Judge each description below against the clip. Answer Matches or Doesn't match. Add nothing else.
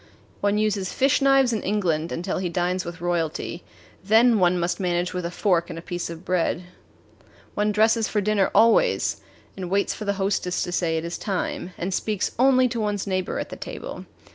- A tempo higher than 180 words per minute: Matches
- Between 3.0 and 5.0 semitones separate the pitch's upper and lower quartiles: Matches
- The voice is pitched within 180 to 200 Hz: Matches